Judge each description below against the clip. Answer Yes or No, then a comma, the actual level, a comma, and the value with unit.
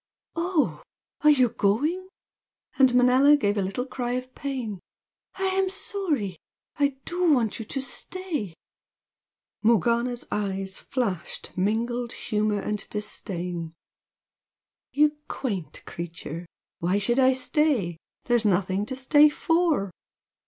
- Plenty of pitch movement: Yes, wide, 6.4 semitones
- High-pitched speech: Yes, high, 240 Hz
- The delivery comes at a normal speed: No, slow, 115 wpm